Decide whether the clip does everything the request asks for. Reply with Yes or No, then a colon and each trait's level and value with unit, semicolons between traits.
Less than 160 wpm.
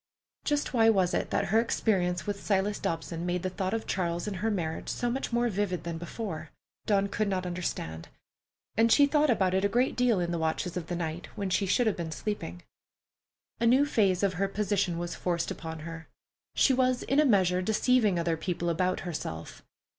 No: fast, 205 wpm